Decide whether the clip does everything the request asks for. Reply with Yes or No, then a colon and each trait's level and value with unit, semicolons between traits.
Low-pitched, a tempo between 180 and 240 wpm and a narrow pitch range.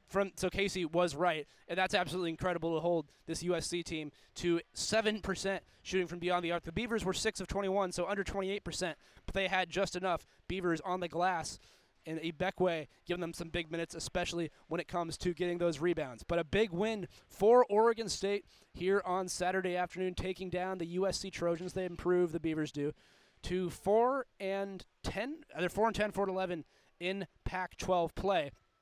No: medium, 180 Hz; average, 185 wpm; narrow, 2.1 semitones